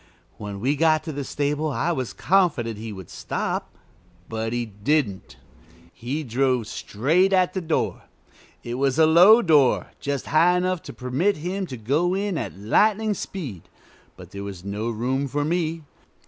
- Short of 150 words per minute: No, average, 165 wpm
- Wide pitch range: Yes, wide, 6.8 semitones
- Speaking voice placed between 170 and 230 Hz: No, medium, 145 Hz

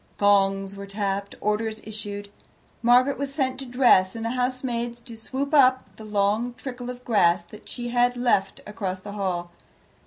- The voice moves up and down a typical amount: Yes, average, 3.8 semitones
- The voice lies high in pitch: Yes, high, 220 Hz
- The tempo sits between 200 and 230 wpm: No, average, 165 wpm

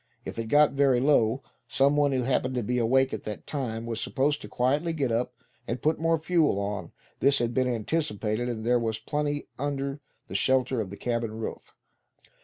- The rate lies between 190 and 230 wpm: Yes, average, 200 wpm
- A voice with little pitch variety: No, average, 3.8 semitones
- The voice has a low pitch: Yes, low, 130 Hz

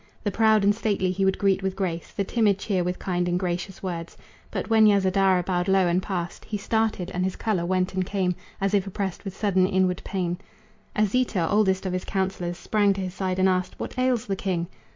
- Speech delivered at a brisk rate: Yes, fast, 215 wpm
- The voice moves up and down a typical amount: No, narrow, 1.8 semitones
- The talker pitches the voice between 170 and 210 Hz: Yes, high, 190 Hz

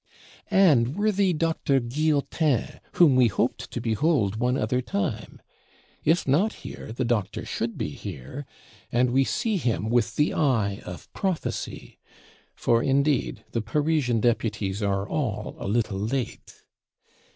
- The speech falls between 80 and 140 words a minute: Yes, slow, 135 wpm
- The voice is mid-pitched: No, low, 125 Hz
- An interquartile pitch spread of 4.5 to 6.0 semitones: Yes, wide, 5.5 semitones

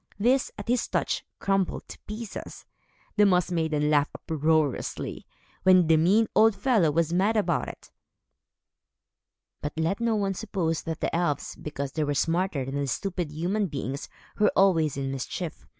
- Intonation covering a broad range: No, average, 4.7 semitones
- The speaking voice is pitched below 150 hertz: No, medium, 170 Hz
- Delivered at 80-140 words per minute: No, average, 155 wpm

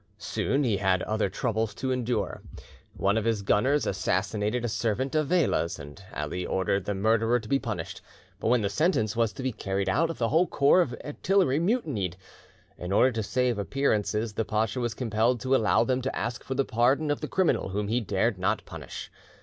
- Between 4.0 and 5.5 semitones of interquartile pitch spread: Yes, average, 4.3 semitones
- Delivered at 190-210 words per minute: Yes, average, 200 wpm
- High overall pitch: No, low, 115 Hz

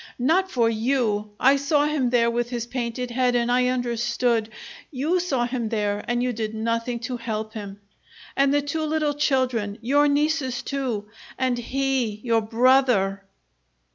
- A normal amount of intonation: Yes, average, 3.0 semitones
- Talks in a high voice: Yes, high, 245 Hz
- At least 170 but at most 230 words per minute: No, average, 160 wpm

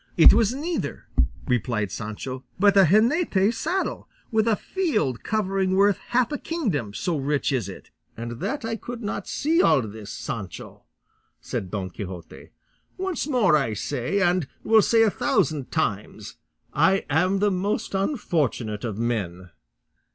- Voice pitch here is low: No, medium, 180 Hz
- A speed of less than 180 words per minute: Yes, average, 150 wpm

